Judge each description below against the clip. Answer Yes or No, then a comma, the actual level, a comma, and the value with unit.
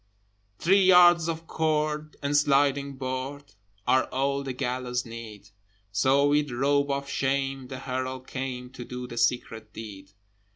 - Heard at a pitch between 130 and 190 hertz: Yes, low, 135 Hz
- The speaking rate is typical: Yes, average, 150 wpm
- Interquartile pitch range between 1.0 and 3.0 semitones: Yes, narrow, 2.4 semitones